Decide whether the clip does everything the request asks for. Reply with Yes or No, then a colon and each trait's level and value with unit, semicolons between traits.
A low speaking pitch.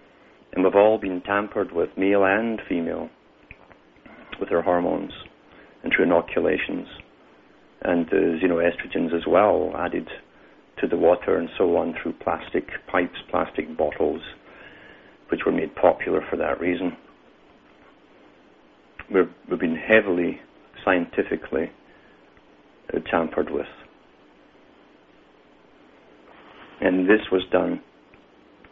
Yes: very low, 95 Hz